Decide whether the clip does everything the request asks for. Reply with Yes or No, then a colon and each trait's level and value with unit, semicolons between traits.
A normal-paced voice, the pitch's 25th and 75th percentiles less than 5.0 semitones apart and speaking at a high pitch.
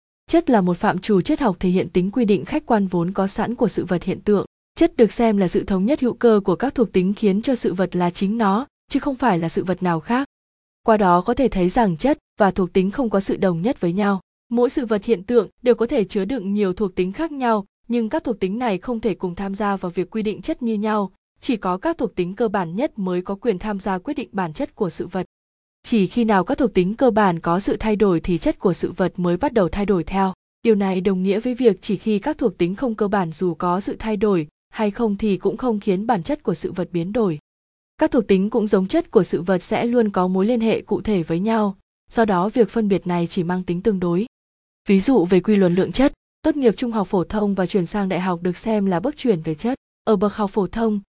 No: fast, 275 wpm; average, 4.0 semitones; high, 205 Hz